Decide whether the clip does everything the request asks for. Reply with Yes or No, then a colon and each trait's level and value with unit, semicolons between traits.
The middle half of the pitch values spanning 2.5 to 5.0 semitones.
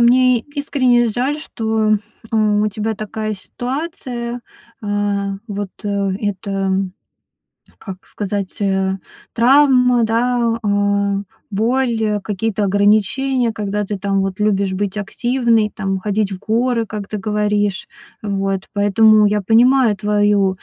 Yes: average, 2.8 semitones